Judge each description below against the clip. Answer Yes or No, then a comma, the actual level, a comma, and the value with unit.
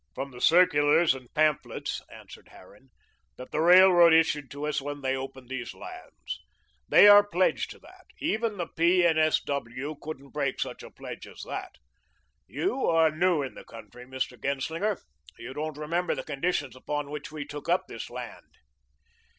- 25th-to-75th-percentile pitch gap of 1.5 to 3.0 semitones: No, average, 4.2 semitones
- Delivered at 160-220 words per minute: Yes, average, 175 wpm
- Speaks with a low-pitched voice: No, medium, 150 Hz